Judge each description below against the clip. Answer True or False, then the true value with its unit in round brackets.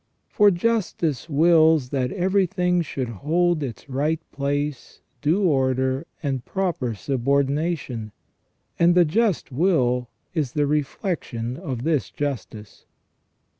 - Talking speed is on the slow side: True (110 wpm)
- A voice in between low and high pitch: True (145 Hz)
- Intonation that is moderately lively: True (4.8 semitones)